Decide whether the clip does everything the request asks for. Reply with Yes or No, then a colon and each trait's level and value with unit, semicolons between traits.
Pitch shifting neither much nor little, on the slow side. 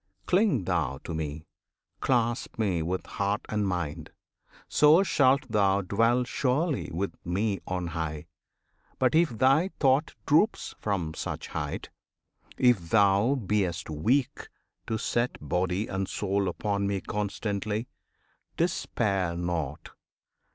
No: wide, 5.9 semitones; slow, 120 wpm